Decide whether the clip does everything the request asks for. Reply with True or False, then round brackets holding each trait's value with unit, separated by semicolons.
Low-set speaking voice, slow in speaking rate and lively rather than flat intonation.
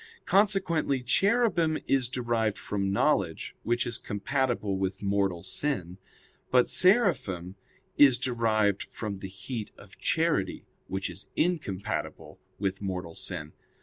True (110 Hz; 115 wpm; 6.2 semitones)